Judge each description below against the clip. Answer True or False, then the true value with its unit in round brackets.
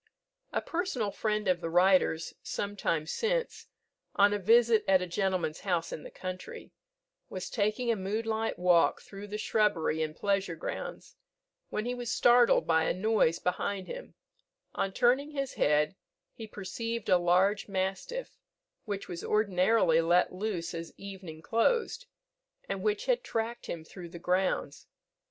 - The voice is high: True (195 Hz)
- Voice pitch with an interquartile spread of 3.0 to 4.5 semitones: True (4.0 semitones)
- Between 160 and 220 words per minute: False (150 wpm)